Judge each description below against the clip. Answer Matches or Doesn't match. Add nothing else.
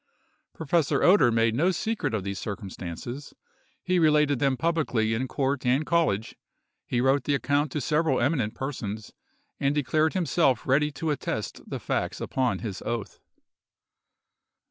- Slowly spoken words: Doesn't match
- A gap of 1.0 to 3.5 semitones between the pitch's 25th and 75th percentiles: Doesn't match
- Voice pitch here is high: Doesn't match